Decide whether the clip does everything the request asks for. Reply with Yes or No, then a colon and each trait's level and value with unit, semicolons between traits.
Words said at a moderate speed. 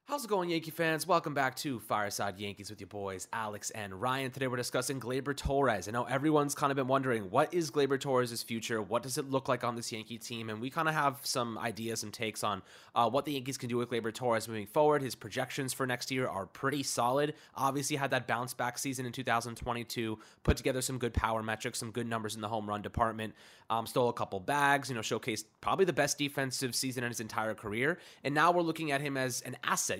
No: fast, 245 wpm